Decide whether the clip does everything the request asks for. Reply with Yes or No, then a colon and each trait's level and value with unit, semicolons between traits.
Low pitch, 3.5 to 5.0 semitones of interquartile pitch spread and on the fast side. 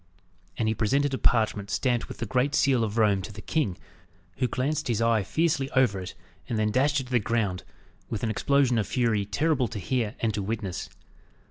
Yes: low, 115 Hz; average, 3.9 semitones; fast, 210 wpm